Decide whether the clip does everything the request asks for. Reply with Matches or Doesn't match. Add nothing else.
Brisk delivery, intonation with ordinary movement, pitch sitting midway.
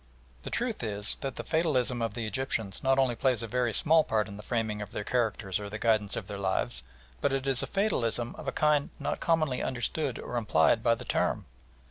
Doesn't match